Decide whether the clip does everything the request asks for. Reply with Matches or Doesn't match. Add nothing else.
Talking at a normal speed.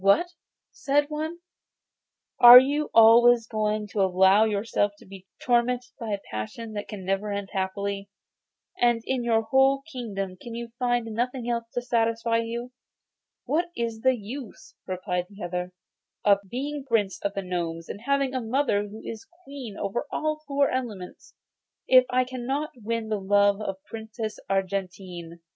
Matches